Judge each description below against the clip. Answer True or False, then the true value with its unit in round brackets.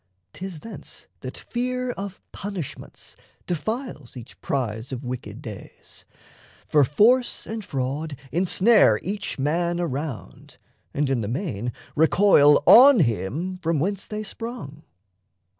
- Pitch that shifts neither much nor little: False (7.2 semitones)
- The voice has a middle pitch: True (165 Hz)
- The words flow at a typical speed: False (120 wpm)